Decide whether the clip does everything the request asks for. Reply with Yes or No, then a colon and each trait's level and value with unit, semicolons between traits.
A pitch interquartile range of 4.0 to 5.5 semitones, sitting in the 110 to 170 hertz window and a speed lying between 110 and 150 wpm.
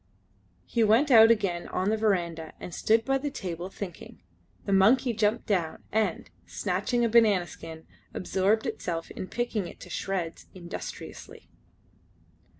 No: average, 4.3 semitones; high, 200 Hz; average, 145 wpm